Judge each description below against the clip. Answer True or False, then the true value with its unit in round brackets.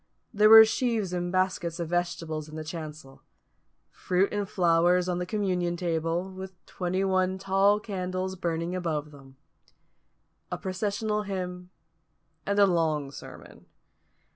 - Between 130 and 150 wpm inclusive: True (135 wpm)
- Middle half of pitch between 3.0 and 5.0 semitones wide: False (2.5 semitones)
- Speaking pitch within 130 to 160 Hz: False (180 Hz)